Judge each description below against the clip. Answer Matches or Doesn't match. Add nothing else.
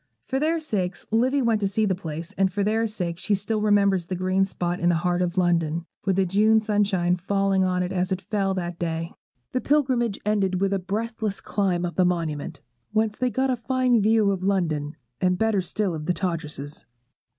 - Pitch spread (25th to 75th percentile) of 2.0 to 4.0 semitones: Matches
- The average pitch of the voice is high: Matches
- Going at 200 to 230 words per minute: Matches